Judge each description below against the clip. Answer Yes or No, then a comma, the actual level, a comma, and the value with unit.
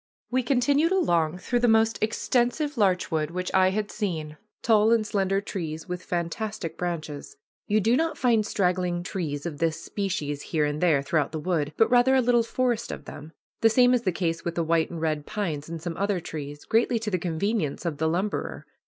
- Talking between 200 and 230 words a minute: Yes, fast, 205 wpm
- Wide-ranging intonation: Yes, wide, 5.7 semitones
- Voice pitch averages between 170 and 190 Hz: Yes, medium, 185 Hz